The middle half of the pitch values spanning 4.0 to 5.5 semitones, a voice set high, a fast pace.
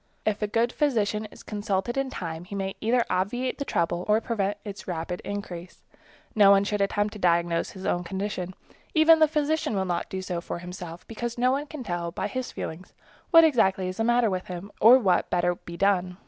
Yes: average, 4.7 semitones; high, 200 Hz; fast, 215 wpm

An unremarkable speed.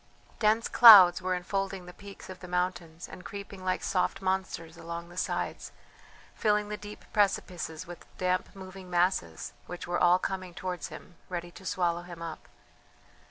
Yes: average, 160 wpm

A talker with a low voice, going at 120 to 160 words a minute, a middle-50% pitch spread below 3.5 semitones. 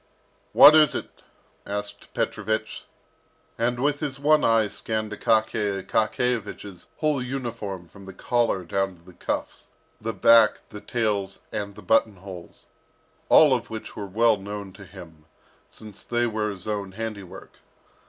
Yes: low, 110 Hz; average, 145 wpm; average, 3.1 semitones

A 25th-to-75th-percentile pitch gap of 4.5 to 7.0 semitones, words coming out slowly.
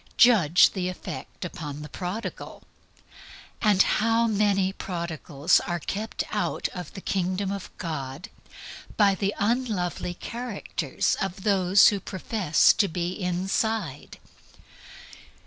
No: average, 3.0 semitones; slow, 115 wpm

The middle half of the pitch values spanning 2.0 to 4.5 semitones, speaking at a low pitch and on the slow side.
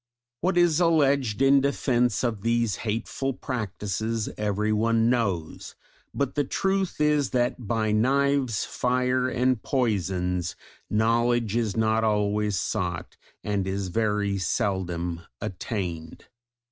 Yes: average, 3.9 semitones; low, 115 Hz; slow, 110 wpm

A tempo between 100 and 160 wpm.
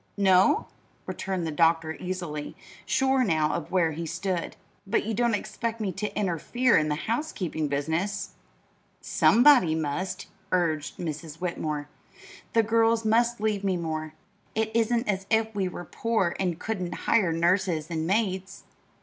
Yes: average, 145 wpm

